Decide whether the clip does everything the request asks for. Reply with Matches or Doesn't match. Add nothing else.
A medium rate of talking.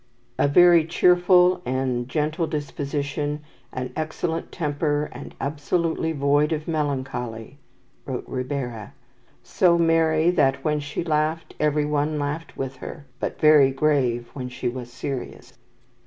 Doesn't match